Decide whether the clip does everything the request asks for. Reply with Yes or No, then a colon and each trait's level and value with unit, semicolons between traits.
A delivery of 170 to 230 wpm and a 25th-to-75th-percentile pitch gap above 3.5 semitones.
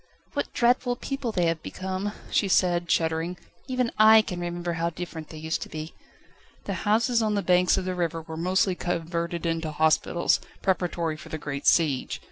No: average, 180 wpm; average, 3.0 semitones